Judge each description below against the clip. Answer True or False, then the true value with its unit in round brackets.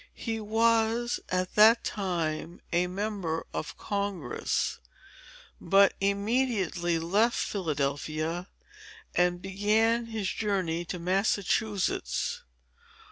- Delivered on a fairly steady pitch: False (4.1 semitones)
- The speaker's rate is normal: False (85 wpm)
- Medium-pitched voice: False (195 Hz)